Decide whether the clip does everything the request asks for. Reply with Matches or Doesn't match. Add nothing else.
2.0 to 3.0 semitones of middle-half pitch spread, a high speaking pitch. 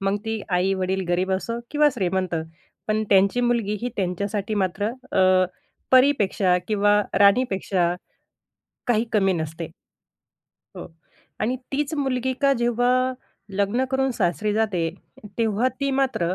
Doesn't match